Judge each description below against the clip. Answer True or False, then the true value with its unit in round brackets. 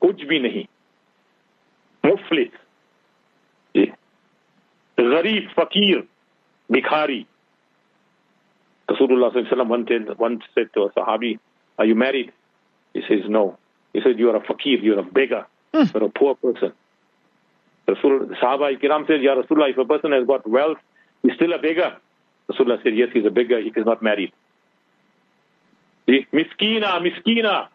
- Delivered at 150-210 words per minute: False (135 wpm)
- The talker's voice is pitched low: False (165 Hz)